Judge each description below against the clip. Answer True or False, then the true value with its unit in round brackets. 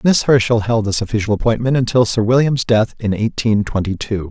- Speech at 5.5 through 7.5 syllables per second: True (5.6 syllables/s)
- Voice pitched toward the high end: False (110 Hz)